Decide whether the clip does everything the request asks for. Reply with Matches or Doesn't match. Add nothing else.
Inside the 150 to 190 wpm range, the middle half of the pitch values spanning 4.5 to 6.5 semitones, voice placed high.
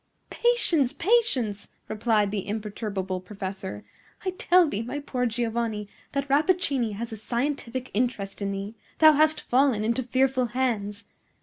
Doesn't match